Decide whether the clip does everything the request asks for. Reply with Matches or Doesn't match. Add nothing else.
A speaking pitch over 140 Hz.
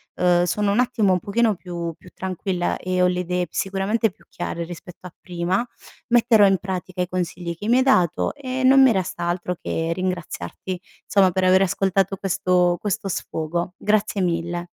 Matches